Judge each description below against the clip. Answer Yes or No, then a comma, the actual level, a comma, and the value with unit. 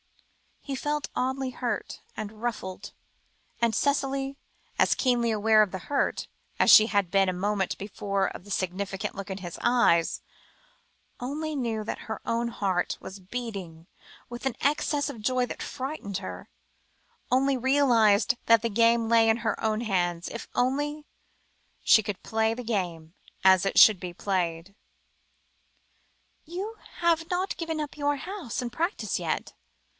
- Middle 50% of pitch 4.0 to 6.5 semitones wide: Yes, average, 5.3 semitones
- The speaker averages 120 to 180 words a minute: Yes, average, 155 wpm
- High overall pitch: Yes, high, 230 Hz